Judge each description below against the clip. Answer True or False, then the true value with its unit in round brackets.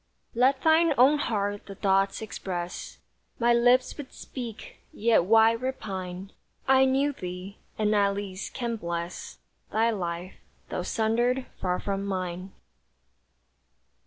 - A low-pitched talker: False (215 Hz)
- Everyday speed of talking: False (125 wpm)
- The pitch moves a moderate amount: True (4.6 semitones)